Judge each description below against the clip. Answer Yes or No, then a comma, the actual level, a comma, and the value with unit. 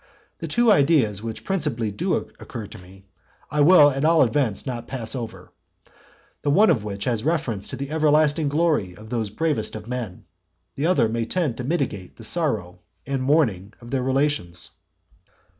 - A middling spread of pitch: No, wide, 5.7 semitones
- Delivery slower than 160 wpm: No, average, 175 wpm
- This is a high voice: No, low, 125 Hz